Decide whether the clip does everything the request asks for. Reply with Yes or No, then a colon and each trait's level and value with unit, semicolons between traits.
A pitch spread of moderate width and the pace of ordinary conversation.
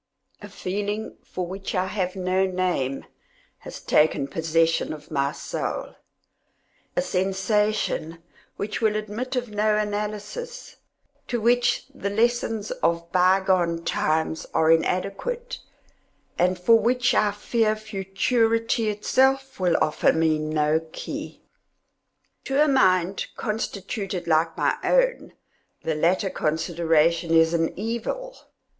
No: average, 4.9 semitones; slow, 115 wpm